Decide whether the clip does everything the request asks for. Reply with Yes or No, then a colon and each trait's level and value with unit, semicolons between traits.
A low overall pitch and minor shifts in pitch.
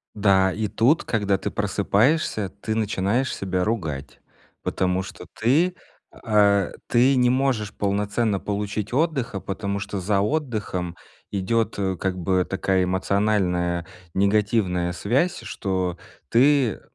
No: low, 100 Hz; average, 3.4 semitones